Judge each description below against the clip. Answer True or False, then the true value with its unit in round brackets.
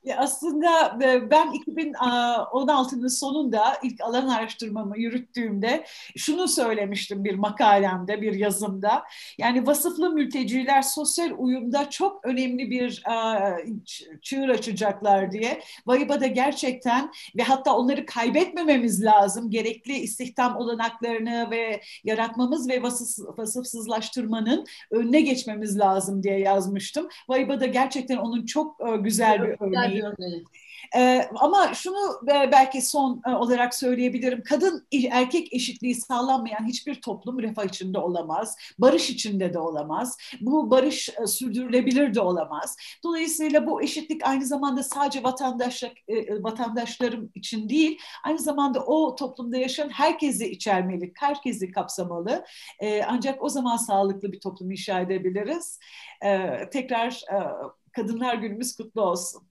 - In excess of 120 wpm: False (115 wpm)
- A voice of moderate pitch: False (245 Hz)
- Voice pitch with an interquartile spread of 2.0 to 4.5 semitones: True (4.2 semitones)